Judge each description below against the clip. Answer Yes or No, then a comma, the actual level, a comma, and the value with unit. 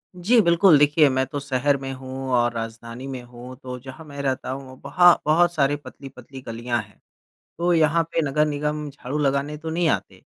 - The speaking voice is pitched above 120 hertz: Yes, medium, 140 Hz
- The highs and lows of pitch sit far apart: No, average, 3.0 semitones